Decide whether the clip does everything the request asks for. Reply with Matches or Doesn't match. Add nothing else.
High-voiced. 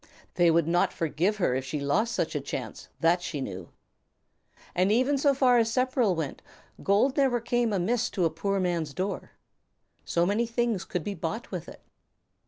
Matches